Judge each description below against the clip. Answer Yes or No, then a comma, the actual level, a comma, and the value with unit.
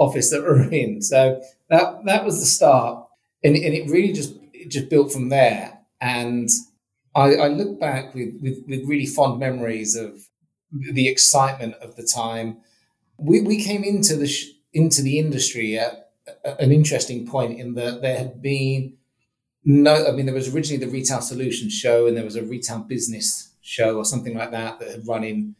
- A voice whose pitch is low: Yes, low, 130 Hz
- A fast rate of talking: No, average, 190 wpm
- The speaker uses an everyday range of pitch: Yes, average, 3.6 semitones